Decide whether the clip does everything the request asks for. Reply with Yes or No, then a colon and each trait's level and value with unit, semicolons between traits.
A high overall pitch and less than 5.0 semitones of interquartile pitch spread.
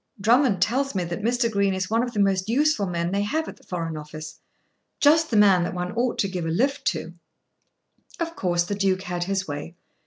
No: high, 195 Hz; average, 5.3 semitones